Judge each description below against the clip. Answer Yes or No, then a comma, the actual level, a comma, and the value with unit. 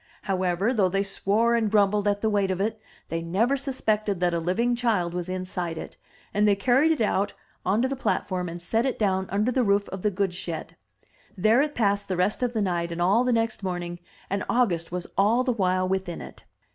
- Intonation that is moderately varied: Yes, average, 3.8 semitones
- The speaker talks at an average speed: No, fast, 220 wpm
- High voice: Yes, high, 200 Hz